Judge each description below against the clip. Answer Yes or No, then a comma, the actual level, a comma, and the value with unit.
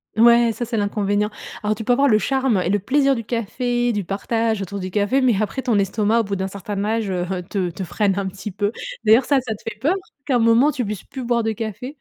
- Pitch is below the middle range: No, high, 220 Hz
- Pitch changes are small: No, average, 3.2 semitones